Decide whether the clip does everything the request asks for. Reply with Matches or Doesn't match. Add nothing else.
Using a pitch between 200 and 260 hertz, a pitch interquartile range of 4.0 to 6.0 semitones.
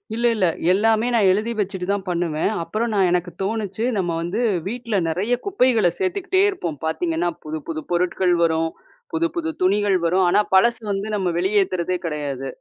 Doesn't match